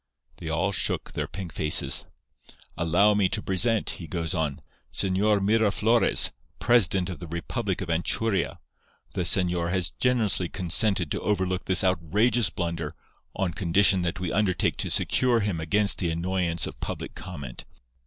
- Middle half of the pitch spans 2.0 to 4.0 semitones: Yes, average, 3.4 semitones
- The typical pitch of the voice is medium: No, very low, 95 Hz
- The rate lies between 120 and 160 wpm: Yes, average, 150 wpm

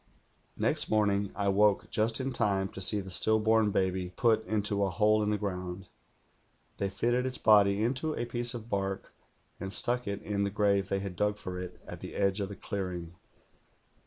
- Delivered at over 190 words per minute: Yes, average, 200 wpm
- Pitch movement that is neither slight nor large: No, narrow, 2.1 semitones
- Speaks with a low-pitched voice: Yes, low, 100 Hz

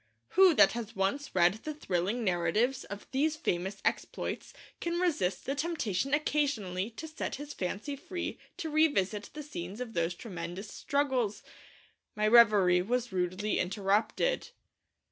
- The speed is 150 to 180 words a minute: No, average, 140 wpm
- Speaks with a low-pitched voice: No, high, 225 Hz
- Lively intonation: Yes, wide, 7.5 semitones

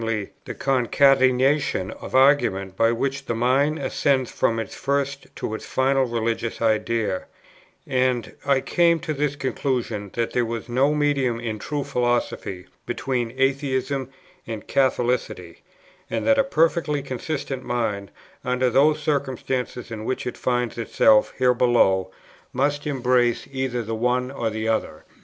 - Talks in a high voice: No, low, 125 Hz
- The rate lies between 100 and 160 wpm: Yes, average, 140 wpm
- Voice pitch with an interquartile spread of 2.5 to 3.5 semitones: Yes, average, 3.0 semitones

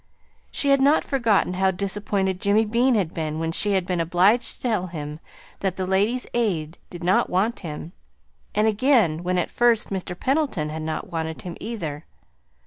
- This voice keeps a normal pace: Yes, average, 180 wpm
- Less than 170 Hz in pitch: No, high, 190 Hz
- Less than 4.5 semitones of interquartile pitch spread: No, average, 4.9 semitones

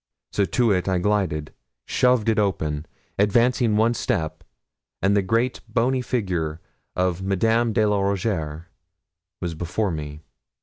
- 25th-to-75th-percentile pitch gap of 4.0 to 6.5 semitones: Yes, average, 4.9 semitones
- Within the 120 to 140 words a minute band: Yes, slow, 135 wpm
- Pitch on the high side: No, low, 100 Hz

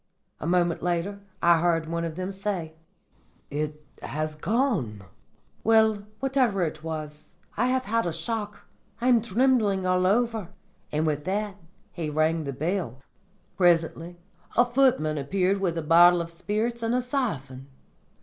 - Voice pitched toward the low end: No, medium, 180 Hz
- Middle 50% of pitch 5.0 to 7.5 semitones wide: Yes, wide, 5.5 semitones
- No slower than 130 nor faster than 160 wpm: Yes, average, 150 wpm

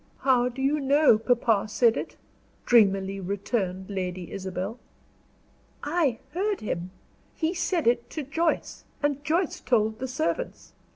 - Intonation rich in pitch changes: Yes, wide, 6.9 semitones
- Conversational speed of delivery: No, slow, 130 wpm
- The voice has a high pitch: Yes, high, 245 Hz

